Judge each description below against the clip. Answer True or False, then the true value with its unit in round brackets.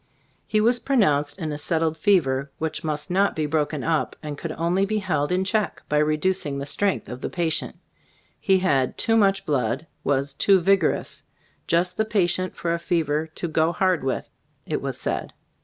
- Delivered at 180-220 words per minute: True (190 wpm)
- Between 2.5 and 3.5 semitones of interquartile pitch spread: False (4.2 semitones)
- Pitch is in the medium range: True (165 Hz)